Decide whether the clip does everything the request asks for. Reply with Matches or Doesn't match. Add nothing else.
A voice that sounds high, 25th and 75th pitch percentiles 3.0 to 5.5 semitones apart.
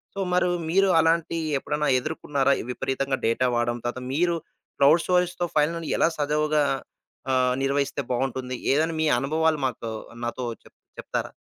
Doesn't match